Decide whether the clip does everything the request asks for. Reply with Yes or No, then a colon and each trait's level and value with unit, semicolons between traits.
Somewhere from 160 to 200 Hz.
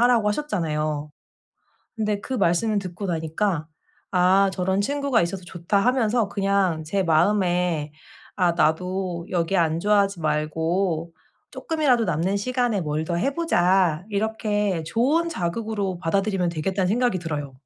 Yes: high, 190 Hz